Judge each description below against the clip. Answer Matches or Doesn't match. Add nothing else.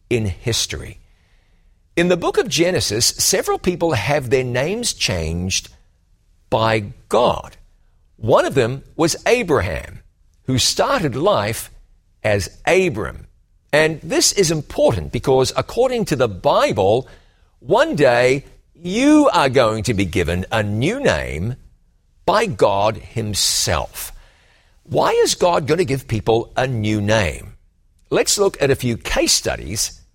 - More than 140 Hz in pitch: Doesn't match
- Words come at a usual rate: Doesn't match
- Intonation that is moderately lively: Doesn't match